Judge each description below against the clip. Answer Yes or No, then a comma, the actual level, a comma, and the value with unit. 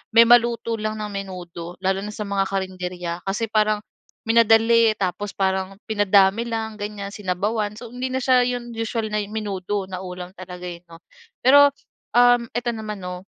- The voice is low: No, high, 210 Hz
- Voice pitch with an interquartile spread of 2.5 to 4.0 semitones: Yes, average, 3.3 semitones